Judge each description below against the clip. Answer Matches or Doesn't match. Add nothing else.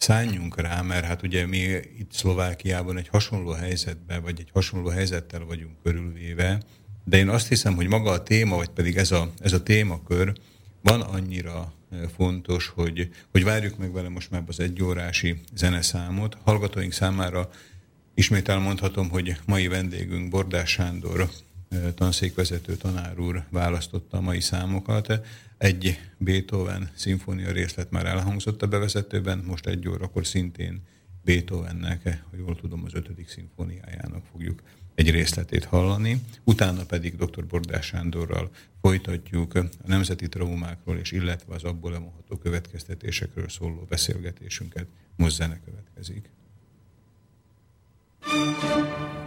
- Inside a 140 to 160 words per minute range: Doesn't match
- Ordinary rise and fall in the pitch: Doesn't match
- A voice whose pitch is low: Matches